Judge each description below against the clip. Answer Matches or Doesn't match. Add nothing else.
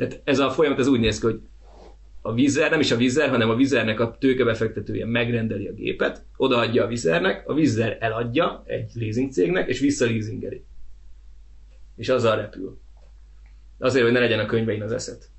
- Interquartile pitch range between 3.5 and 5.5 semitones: Matches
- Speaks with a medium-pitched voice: Doesn't match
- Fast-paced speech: Matches